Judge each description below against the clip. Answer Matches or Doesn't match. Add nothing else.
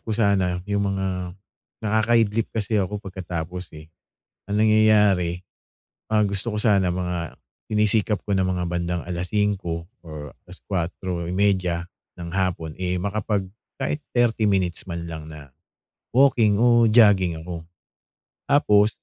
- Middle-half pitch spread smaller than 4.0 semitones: Matches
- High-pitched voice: Doesn't match